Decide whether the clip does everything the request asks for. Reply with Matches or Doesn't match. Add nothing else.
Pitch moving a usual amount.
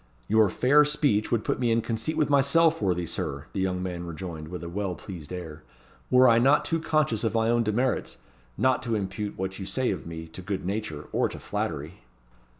Doesn't match